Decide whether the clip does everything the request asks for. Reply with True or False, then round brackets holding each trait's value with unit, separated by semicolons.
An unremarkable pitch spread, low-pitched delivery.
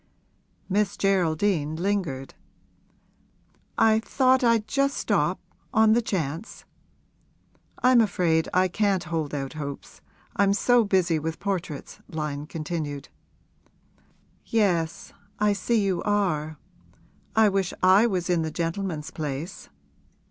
False (4.6 semitones; 185 Hz)